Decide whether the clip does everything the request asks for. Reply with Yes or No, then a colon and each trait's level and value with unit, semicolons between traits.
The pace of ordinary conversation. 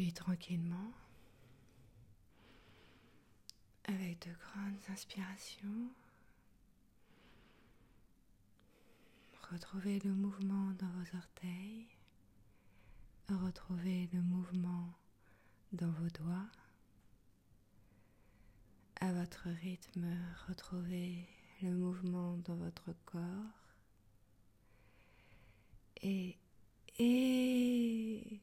No: slow, 60 wpm